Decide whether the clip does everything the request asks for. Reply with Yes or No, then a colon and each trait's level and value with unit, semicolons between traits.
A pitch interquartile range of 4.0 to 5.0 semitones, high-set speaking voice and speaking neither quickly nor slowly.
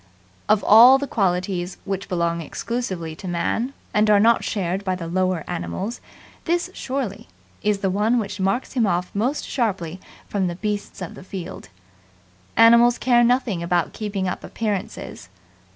Yes: average, 4.4 semitones; high, 200 Hz; average, 155 wpm